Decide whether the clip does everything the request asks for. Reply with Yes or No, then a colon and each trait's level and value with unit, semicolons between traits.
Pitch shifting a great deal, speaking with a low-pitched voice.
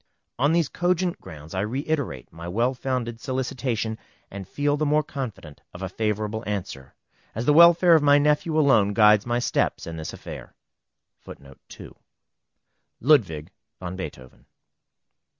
Yes: wide, 7.2 semitones; low, 120 Hz